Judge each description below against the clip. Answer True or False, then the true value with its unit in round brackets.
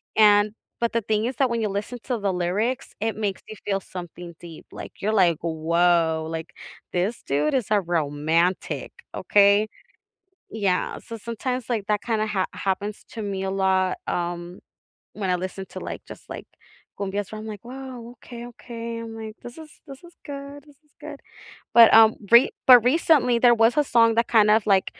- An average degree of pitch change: True (4.0 semitones)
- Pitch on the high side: True (210 Hz)